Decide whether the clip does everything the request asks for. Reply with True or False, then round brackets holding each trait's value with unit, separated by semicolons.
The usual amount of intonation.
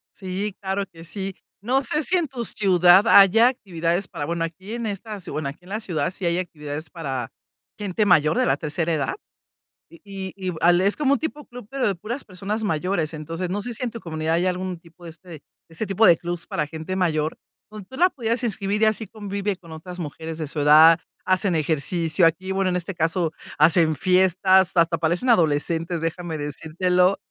True (3.6 semitones)